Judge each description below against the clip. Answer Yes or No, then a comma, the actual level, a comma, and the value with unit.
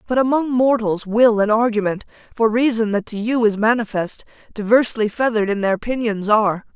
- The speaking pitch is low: No, high, 225 Hz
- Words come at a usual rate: Yes, average, 170 wpm